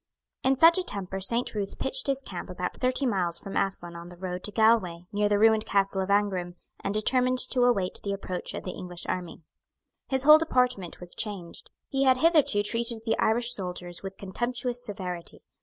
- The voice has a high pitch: Yes, high, 205 Hz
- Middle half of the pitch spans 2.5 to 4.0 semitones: No, average, 5.2 semitones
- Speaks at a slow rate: No, average, 190 wpm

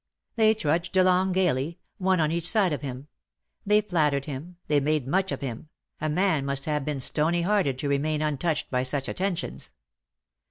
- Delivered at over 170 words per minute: Yes, average, 185 wpm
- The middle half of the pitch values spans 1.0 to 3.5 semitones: No, average, 4.6 semitones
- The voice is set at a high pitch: No, medium, 155 Hz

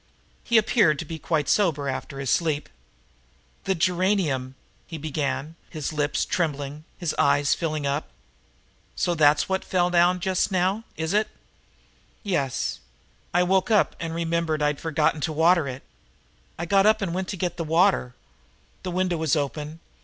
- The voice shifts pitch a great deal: No, average, 3.8 semitones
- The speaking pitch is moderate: Yes, medium, 165 Hz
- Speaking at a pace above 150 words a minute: Yes, average, 165 wpm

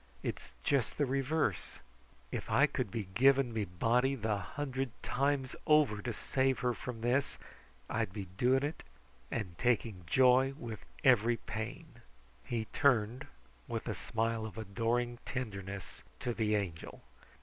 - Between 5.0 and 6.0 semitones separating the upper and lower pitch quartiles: No, average, 3.5 semitones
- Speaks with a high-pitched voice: No, low, 120 Hz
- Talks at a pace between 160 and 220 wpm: No, average, 140 wpm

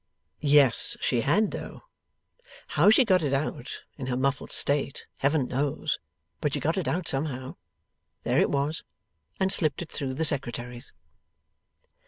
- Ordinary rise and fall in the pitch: Yes, average, 3.4 semitones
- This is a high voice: No, medium, 140 Hz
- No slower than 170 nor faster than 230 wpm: No, average, 150 wpm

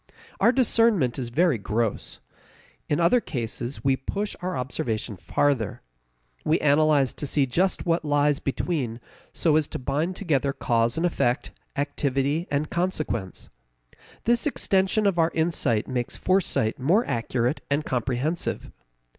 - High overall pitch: No, medium, 145 Hz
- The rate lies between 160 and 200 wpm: No, slow, 135 wpm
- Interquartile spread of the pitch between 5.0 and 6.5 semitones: Yes, wide, 5.5 semitones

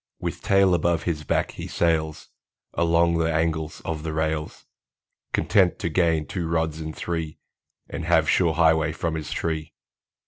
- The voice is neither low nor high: No, very low, 80 Hz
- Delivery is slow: No, average, 160 wpm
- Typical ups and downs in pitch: No, narrow, 1.3 semitones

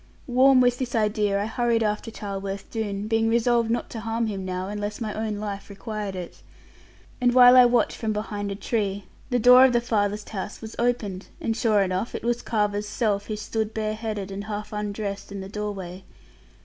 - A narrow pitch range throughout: Yes, narrow, 2.3 semitones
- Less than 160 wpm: No, average, 195 wpm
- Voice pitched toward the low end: No, high, 215 Hz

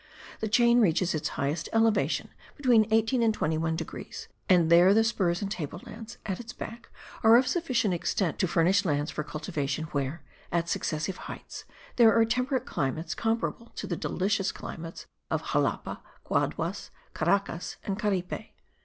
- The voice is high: Yes, high, 195 Hz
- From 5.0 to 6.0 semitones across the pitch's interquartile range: Yes, wide, 5.4 semitones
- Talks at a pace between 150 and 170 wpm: Yes, average, 155 wpm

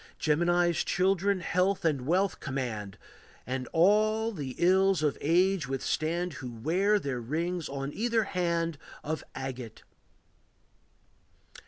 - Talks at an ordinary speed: No, slow, 115 wpm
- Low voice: No, medium, 170 Hz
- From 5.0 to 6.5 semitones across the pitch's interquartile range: Yes, wide, 5.5 semitones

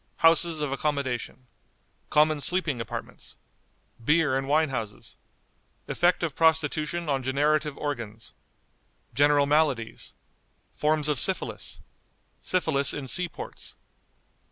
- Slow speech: Yes, slow, 105 wpm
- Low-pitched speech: No, medium, 150 Hz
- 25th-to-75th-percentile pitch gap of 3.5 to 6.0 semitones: No, average, 2.9 semitones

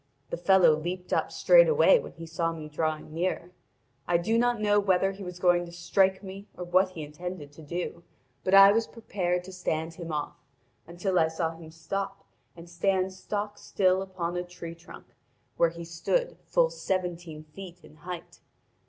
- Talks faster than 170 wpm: Yes, average, 180 wpm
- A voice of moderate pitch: Yes, medium, 180 Hz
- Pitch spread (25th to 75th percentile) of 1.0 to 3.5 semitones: Yes, narrow, 2.5 semitones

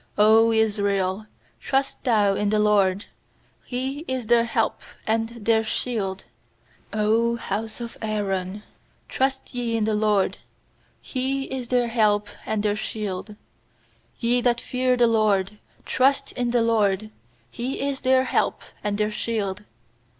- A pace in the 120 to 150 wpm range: Yes, slow, 135 wpm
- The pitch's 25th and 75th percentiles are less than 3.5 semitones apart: Yes, average, 2.8 semitones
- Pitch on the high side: Yes, high, 220 Hz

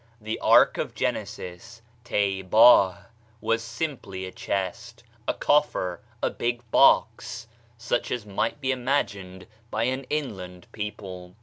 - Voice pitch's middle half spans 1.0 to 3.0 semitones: No, average, 4.4 semitones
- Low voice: Yes, low, 110 Hz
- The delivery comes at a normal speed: No, slow, 120 wpm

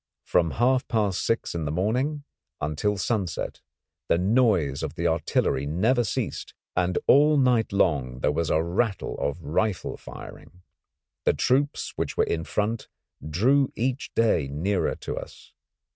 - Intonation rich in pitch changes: Yes, wide, 6.7 semitones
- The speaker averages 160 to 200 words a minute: No, average, 145 wpm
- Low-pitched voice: Yes, very low, 95 Hz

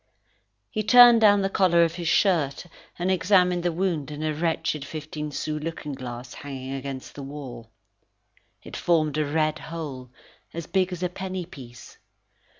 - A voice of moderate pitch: Yes, medium, 160 Hz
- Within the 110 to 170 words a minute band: Yes, average, 160 wpm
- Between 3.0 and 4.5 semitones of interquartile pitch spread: Yes, average, 4.0 semitones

